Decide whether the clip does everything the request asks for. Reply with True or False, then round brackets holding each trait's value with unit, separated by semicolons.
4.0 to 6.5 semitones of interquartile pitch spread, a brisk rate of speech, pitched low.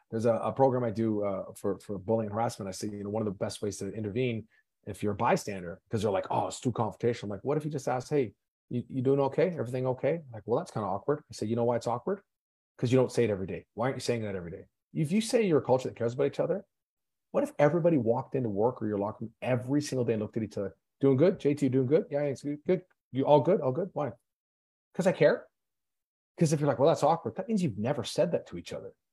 True (4.8 semitones; 285 wpm; 125 Hz)